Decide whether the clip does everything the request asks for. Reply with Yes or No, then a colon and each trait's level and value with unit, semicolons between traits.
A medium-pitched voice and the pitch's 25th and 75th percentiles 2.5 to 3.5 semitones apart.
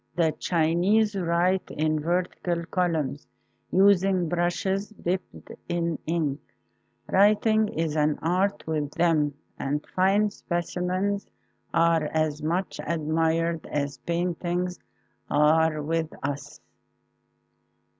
Yes: medium, 170 Hz; average, 2.8 semitones